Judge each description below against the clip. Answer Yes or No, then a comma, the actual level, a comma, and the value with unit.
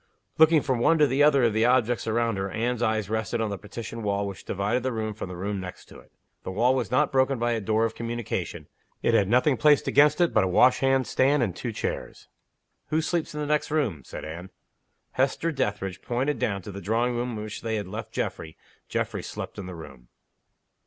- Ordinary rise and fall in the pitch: Yes, average, 4.4 semitones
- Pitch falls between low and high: No, low, 115 Hz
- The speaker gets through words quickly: Yes, fast, 225 wpm